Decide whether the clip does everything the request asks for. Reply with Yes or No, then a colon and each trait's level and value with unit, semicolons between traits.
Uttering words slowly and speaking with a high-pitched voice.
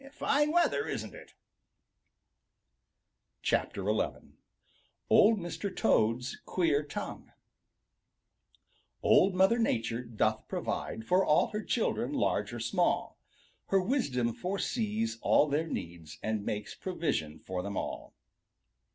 No: slow, 110 wpm; medium, 155 Hz